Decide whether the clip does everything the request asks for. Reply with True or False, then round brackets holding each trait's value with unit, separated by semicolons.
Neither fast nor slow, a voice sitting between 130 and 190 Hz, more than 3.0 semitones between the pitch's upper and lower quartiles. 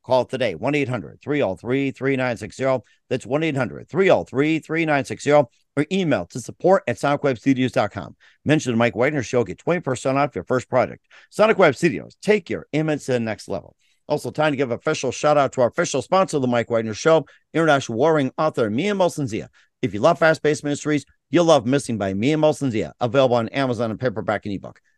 True (185 wpm; 135 Hz; 3.8 semitones)